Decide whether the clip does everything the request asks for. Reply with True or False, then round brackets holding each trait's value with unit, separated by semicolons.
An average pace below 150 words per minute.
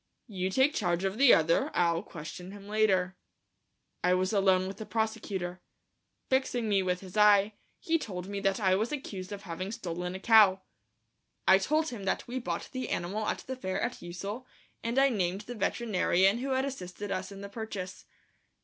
False (185 wpm)